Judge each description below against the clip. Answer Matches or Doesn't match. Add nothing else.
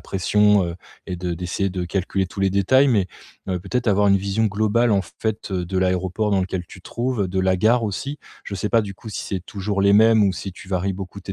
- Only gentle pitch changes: Matches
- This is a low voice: Matches